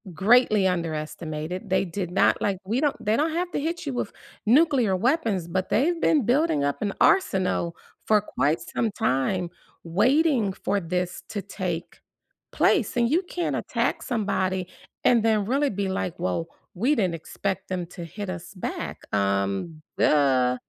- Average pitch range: No, wide, 6.1 semitones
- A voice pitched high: Yes, high, 195 Hz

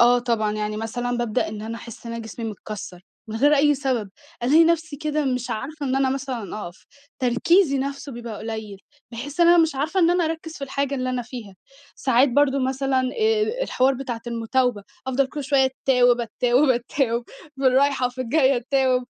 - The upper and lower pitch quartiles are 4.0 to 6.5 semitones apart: No, average, 3.1 semitones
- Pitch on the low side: No, very high, 260 Hz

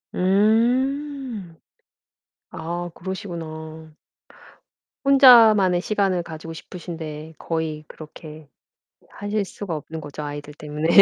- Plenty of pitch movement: No, average, 4.7 semitones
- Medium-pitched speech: Yes, medium, 170 Hz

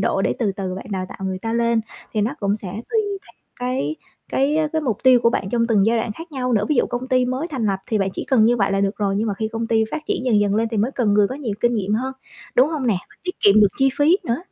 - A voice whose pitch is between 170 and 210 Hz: No, high, 230 Hz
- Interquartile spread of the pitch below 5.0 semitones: Yes, average, 3.9 semitones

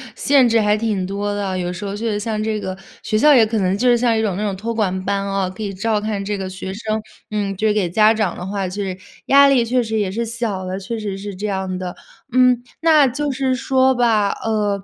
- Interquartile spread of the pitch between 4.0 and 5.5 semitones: No, average, 3.0 semitones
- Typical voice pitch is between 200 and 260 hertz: Yes, high, 210 Hz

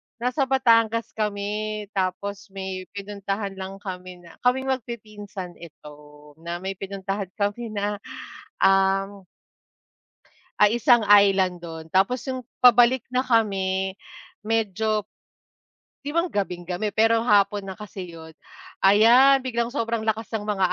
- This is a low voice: No, high, 205 Hz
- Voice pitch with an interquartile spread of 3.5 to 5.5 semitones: No, average, 3.1 semitones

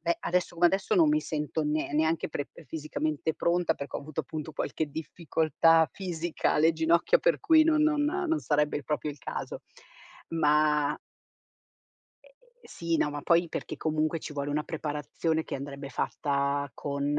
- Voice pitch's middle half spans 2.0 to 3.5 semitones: Yes, narrow, 2.5 semitones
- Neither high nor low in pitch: Yes, medium, 155 Hz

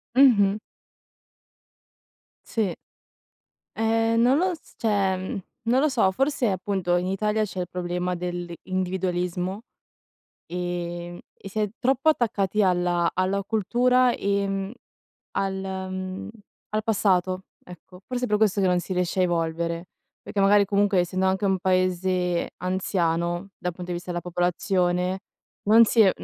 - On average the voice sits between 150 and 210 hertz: Yes, high, 190 Hz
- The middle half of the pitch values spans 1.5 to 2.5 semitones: No, average, 2.9 semitones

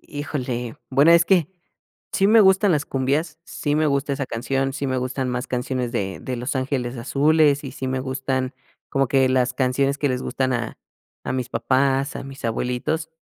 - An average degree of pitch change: No, narrow, 2.1 semitones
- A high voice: No, low, 135 Hz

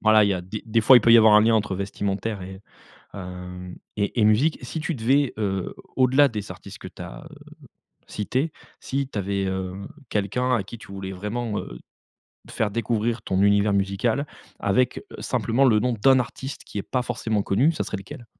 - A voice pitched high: No, low, 105 Hz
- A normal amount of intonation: Yes, average, 3.7 semitones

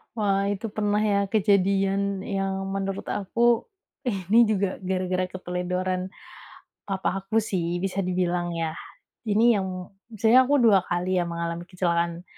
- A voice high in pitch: Yes, high, 195 Hz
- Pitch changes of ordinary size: No, narrow, 2.2 semitones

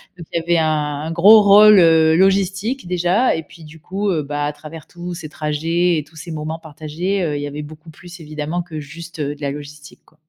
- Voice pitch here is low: No, medium, 160 Hz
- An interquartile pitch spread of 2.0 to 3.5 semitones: Yes, average, 2.8 semitones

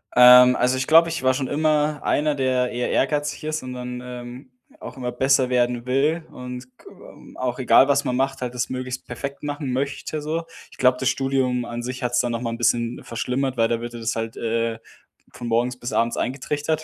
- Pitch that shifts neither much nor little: No, narrow, 2.1 semitones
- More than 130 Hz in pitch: No, low, 125 Hz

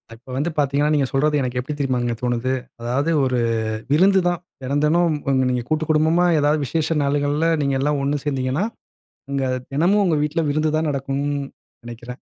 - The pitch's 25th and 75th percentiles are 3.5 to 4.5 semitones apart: No, average, 3.0 semitones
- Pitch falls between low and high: Yes, medium, 145 Hz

